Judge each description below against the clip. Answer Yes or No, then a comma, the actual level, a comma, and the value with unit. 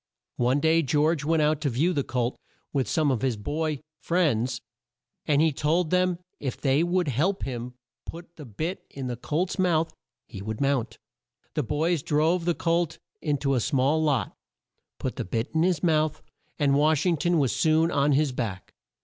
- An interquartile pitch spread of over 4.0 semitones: No, average, 3.7 semitones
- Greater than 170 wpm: Yes, average, 190 wpm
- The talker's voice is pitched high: No, medium, 150 Hz